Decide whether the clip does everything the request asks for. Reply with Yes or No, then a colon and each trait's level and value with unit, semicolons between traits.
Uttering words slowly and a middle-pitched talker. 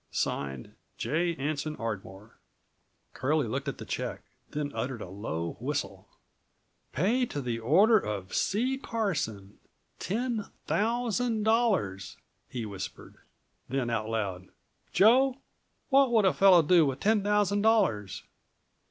Yes: slow, 115 wpm; medium, 155 Hz